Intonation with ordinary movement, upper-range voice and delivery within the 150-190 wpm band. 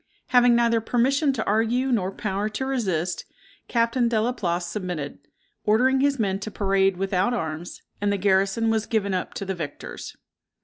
Yes: average, 3.8 semitones; high, 210 Hz; average, 170 wpm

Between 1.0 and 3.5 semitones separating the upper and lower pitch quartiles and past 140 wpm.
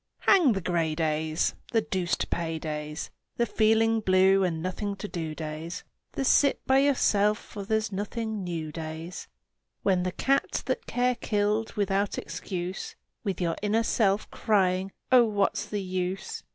No: average, 4.1 semitones; average, 155 wpm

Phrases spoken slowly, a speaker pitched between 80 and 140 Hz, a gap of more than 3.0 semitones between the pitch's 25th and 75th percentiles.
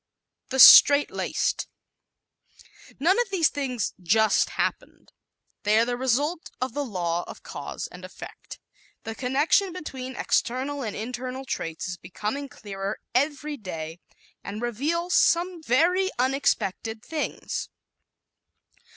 No: slow, 125 wpm; very high, 260 Hz; average, 5.3 semitones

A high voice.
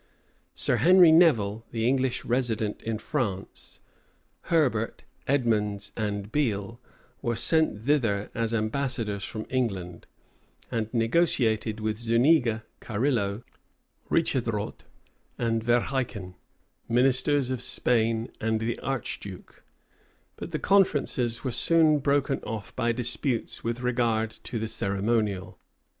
No: low, 115 Hz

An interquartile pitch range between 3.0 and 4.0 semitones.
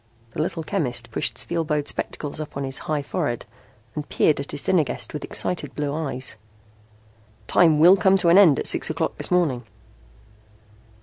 Yes: average, 3.6 semitones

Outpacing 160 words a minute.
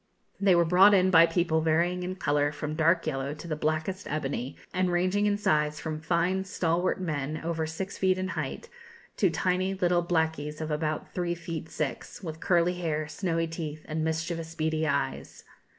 Yes: average, 180 wpm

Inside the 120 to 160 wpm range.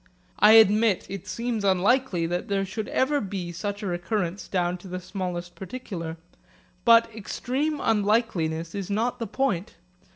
Yes: average, 150 wpm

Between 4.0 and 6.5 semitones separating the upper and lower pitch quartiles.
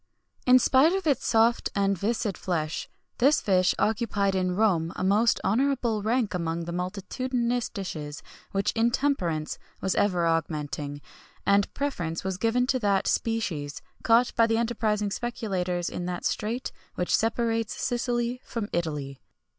Yes: average, 4.9 semitones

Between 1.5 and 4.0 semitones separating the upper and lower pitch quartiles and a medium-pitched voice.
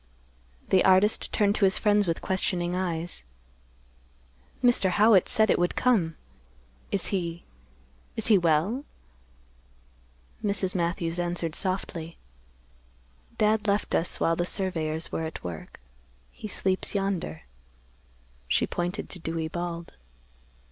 Yes: average, 3.3 semitones; medium, 180 Hz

